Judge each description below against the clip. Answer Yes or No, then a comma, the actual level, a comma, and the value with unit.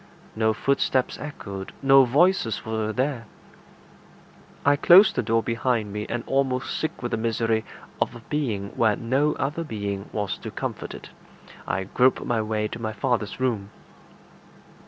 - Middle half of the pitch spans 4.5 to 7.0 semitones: No, average, 3.8 semitones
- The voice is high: No, low, 115 Hz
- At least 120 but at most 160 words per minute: Yes, average, 155 wpm